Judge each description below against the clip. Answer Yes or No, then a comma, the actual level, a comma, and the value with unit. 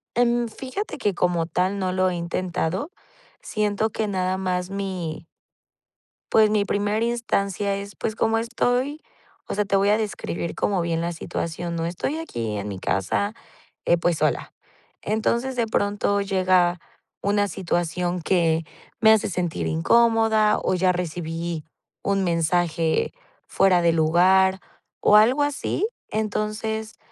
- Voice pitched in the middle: No, high, 195 Hz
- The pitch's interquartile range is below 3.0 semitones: No, average, 3.8 semitones